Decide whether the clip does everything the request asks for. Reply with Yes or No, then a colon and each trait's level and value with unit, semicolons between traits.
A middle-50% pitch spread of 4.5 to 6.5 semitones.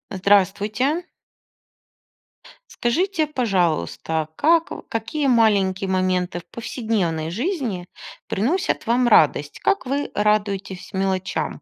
Yes: average, 5.3 semitones